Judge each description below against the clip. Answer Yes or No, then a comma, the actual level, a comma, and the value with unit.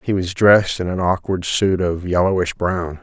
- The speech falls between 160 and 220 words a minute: Yes, average, 200 wpm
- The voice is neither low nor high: No, very low, 90 Hz